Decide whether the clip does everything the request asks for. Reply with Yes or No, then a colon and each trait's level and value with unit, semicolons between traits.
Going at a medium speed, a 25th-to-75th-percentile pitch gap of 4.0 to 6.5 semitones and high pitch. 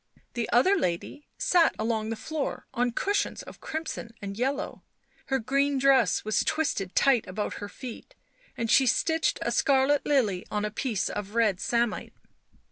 Yes: average, 160 wpm; average, 4.6 semitones; high, 240 Hz